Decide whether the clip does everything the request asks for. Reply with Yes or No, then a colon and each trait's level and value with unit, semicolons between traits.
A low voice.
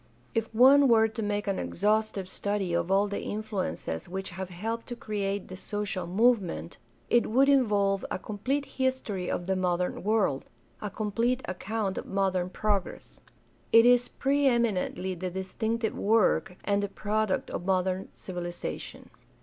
No: high, 205 Hz